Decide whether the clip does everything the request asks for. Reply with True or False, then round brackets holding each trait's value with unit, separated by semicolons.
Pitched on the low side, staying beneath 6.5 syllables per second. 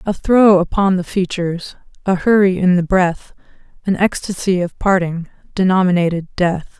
False (185 Hz; 4.9 syllables/s)